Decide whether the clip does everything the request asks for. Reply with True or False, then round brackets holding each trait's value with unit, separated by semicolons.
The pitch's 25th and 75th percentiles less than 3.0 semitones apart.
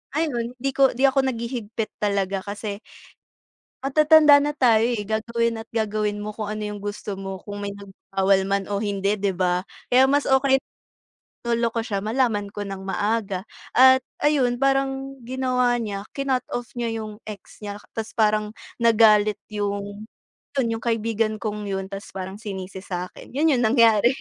False (3.4 semitones)